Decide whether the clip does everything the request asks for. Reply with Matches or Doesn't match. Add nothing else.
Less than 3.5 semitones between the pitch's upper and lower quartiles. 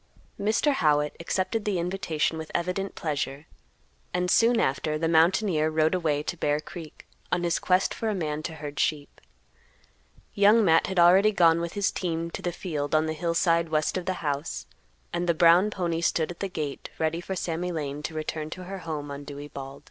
Matches